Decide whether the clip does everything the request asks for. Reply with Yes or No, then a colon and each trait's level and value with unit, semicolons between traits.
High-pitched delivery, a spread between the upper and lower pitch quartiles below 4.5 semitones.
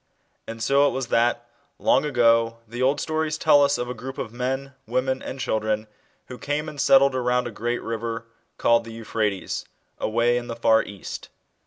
No: low, 120 Hz; average, 2.7 semitones